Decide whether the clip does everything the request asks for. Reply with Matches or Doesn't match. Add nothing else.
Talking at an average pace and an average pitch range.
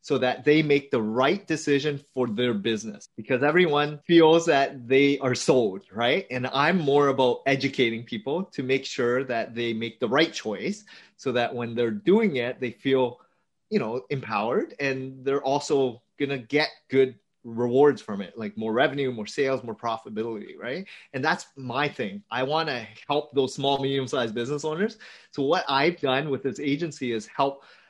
Matches